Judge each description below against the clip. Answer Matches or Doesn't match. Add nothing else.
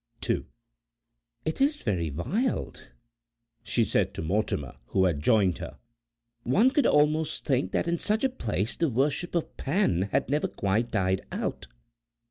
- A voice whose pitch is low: Matches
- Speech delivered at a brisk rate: Doesn't match